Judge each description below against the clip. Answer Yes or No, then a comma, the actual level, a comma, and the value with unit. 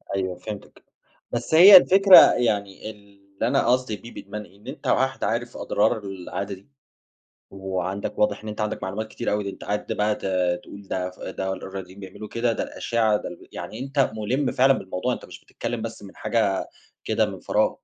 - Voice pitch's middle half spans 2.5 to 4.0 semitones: Yes, average, 3.2 semitones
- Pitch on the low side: Yes, low, 105 Hz